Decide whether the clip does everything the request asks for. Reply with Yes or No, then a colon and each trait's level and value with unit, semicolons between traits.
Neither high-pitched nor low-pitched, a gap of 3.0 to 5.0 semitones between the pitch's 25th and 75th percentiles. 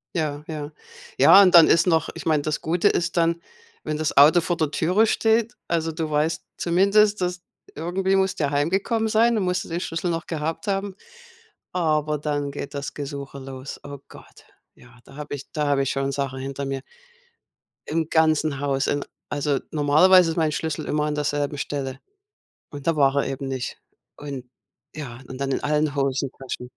Yes: medium, 150 Hz; average, 3.3 semitones